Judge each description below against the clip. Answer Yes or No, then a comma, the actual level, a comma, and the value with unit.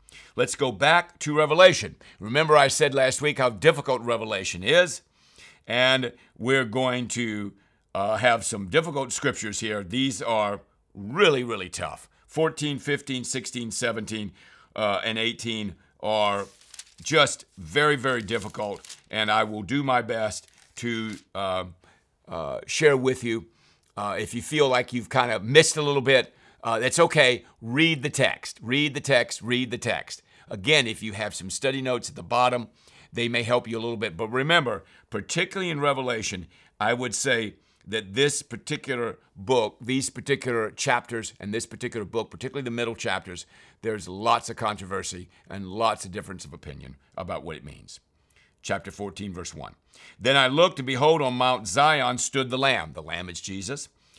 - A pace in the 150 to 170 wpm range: Yes, average, 165 wpm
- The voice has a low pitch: Yes, low, 120 Hz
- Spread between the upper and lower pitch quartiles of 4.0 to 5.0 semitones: Yes, average, 4.7 semitones